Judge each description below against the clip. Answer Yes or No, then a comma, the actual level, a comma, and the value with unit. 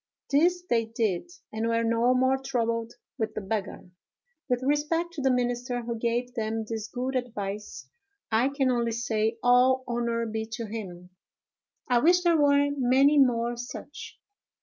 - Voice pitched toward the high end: Yes, high, 240 Hz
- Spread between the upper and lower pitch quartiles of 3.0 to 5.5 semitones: No, narrow, 2.6 semitones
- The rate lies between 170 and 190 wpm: No, average, 155 wpm